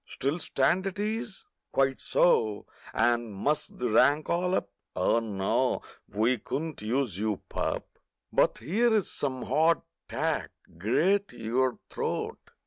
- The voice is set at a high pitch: No, low, 135 Hz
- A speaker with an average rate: No, slow, 125 wpm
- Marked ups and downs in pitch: Yes, wide, 7.8 semitones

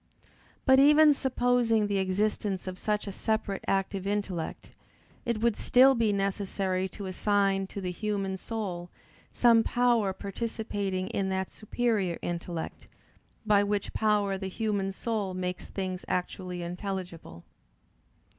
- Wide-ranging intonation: No, average, 2.7 semitones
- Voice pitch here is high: Yes, high, 200 Hz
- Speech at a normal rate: No, slow, 125 wpm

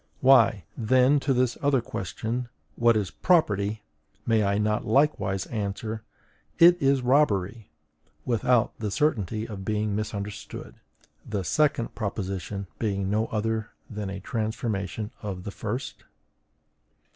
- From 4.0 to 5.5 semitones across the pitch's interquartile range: No, average, 3.6 semitones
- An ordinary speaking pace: No, slow, 120 wpm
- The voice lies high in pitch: No, low, 110 Hz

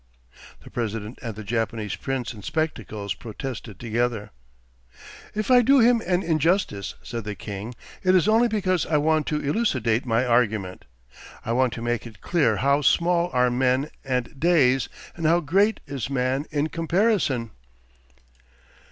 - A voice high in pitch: No, low, 130 Hz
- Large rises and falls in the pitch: Yes, wide, 6.5 semitones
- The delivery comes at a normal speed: Yes, average, 150 wpm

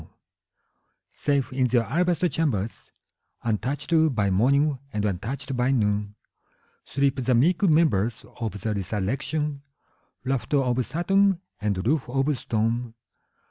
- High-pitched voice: No, low, 130 Hz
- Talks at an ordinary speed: No, slow, 120 wpm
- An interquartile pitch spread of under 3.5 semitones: No, average, 5.0 semitones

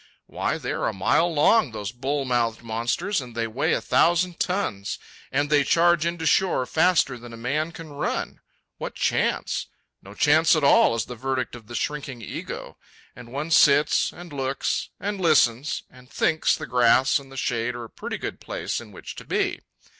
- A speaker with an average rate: Yes, average, 190 wpm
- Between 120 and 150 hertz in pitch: Yes, low, 135 Hz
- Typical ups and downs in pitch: Yes, average, 4.9 semitones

